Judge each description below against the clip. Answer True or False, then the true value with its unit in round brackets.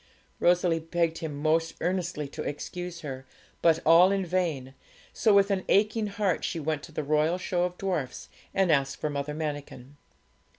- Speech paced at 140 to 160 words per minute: False (170 wpm)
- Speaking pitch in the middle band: True (165 Hz)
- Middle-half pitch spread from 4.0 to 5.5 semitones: False (3.4 semitones)